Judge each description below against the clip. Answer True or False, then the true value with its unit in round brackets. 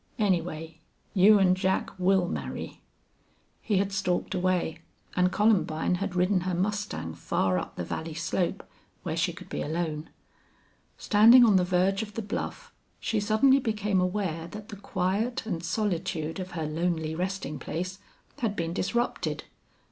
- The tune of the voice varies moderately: True (3.5 semitones)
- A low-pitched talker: False (185 Hz)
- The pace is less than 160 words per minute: True (150 wpm)